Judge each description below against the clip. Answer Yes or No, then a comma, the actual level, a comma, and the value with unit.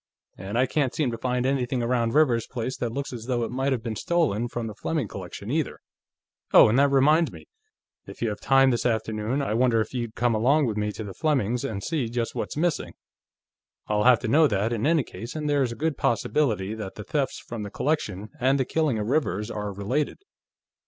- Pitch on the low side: Yes, low, 120 Hz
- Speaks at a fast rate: Yes, fast, 220 wpm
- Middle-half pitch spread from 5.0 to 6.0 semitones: No, average, 4.1 semitones